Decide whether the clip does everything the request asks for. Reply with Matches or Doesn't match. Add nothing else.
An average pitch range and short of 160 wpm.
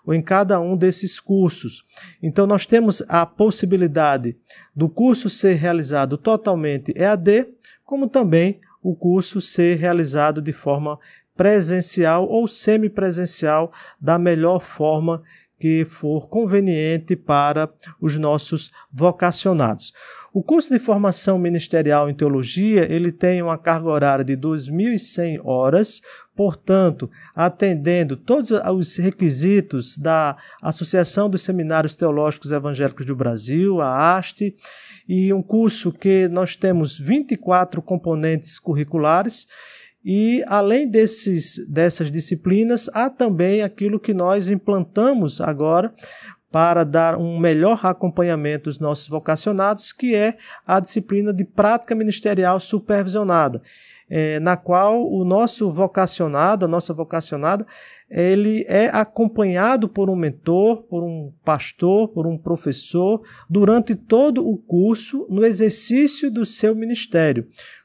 Matches